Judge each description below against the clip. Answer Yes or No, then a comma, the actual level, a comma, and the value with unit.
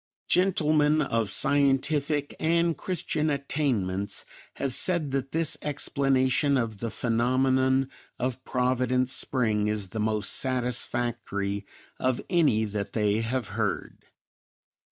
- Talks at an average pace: No, slow, 110 wpm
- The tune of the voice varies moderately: Yes, average, 4.2 semitones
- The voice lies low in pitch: Yes, low, 130 Hz